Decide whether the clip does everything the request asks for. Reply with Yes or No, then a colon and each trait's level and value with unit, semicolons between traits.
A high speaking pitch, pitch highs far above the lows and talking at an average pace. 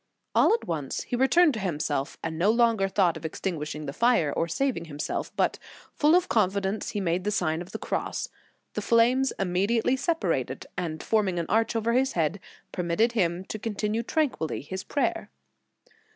Yes: high, 195 Hz; wide, 5.7 semitones; average, 175 wpm